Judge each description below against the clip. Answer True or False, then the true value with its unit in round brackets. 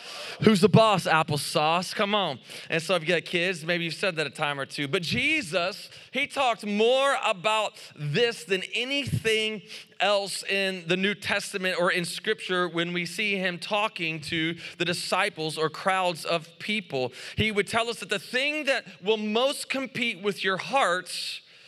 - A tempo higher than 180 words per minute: False (175 wpm)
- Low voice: False (190 Hz)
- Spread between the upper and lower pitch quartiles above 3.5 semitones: True (4.3 semitones)